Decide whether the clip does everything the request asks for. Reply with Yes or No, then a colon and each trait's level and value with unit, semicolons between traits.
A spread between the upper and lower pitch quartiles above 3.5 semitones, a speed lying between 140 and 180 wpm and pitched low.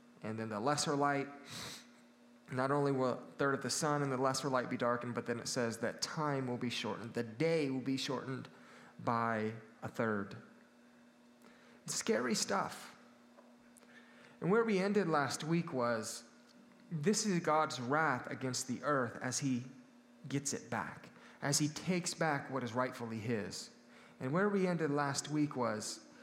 Yes: average, 3.9 semitones; average, 165 wpm; low, 130 Hz